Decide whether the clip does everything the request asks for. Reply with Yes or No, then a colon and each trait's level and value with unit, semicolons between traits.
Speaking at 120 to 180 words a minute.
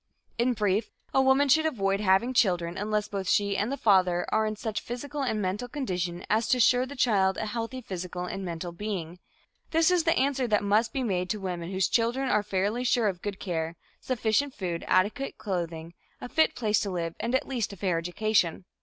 No: fast, 205 wpm